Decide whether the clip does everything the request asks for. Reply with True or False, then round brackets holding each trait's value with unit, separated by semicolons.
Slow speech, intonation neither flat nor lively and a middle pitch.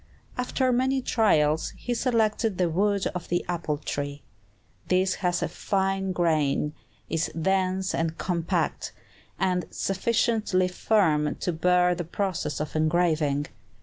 True (125 wpm; 3.4 semitones; 180 Hz)